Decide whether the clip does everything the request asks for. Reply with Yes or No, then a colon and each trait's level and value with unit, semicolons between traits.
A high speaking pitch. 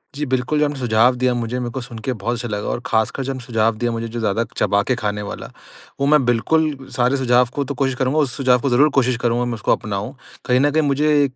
No: low, 125 Hz